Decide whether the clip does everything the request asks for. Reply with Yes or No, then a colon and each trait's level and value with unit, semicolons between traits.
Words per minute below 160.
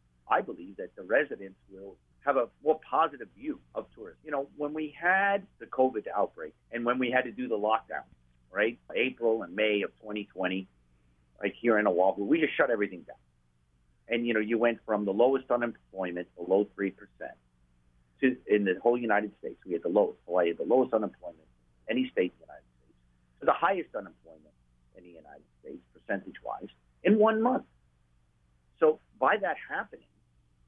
No: average, 185 wpm